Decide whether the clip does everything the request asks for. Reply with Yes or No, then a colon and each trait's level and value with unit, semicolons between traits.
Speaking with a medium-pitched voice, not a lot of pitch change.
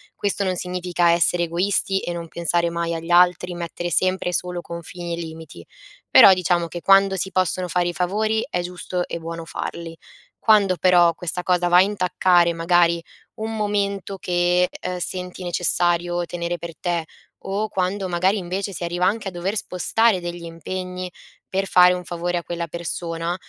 Yes: medium, 180 Hz; narrow, 1.4 semitones